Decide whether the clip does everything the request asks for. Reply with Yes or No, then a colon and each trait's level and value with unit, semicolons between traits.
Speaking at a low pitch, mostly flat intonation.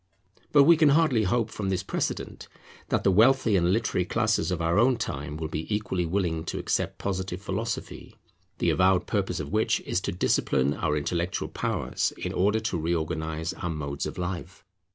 No: very low, 95 Hz; average, 4.7 semitones